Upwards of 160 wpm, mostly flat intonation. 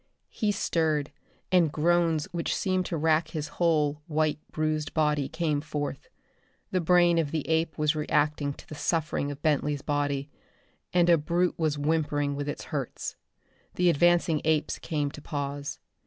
No: average, 155 wpm; narrow, 2.3 semitones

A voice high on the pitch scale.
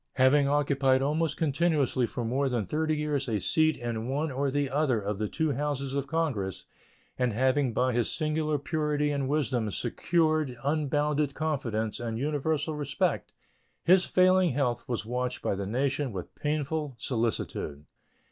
No: medium, 140 Hz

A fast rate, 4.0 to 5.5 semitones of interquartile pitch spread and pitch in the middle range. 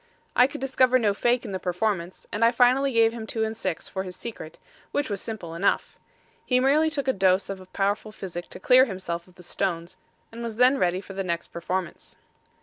No: fast, 215 wpm; average, 5.1 semitones; high, 210 Hz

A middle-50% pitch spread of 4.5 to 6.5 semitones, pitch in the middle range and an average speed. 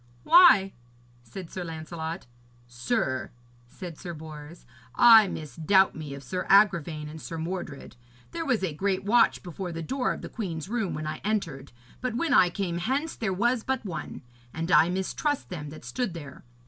Yes: wide, 5.4 semitones; medium, 180 Hz; average, 175 wpm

